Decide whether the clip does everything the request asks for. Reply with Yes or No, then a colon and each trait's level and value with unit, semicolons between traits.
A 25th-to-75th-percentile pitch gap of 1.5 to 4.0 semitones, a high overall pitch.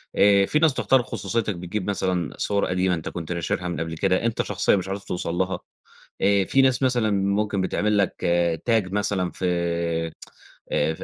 No: average, 3.0 semitones; very low, 95 Hz